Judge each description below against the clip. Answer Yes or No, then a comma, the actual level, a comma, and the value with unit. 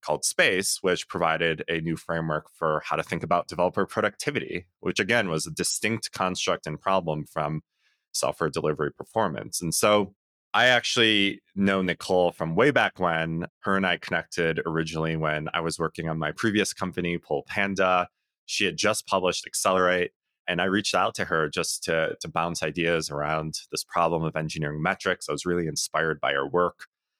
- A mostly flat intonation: Yes, narrow, 2.3 semitones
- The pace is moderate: Yes, average, 175 wpm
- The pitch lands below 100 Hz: Yes, very low, 85 Hz